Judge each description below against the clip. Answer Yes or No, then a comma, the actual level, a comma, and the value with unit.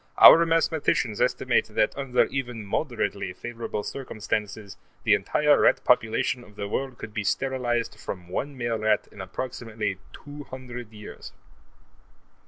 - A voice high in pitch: No, low, 115 Hz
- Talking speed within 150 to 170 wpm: No, slow, 135 wpm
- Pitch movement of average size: Yes, average, 3.9 semitones